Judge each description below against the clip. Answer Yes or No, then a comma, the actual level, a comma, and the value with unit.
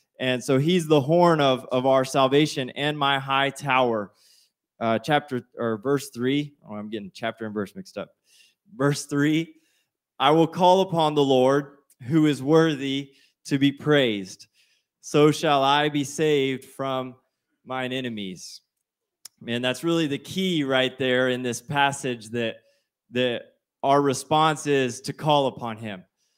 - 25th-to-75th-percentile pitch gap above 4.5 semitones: No, average, 2.8 semitones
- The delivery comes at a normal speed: Yes, average, 150 wpm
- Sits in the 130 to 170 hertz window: Yes, low, 135 Hz